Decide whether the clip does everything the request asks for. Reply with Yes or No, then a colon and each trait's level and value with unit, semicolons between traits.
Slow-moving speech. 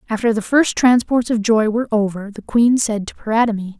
No: fast, 205 wpm